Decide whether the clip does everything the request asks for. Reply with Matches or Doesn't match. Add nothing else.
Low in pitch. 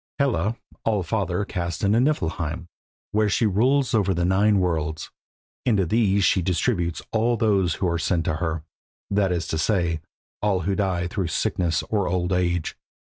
Matches